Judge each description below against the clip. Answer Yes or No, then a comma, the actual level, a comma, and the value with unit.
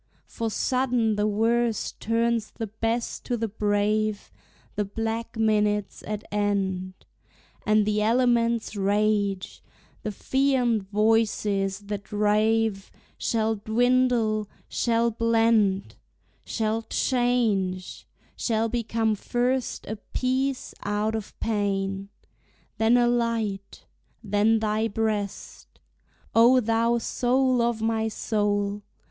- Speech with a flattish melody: Yes, narrow, 2.0 semitones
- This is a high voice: Yes, high, 220 Hz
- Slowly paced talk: Yes, slow, 105 wpm